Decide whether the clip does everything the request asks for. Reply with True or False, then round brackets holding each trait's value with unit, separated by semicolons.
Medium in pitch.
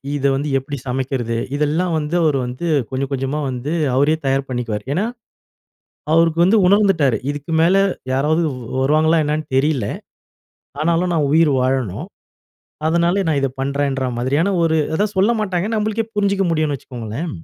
True (150 Hz)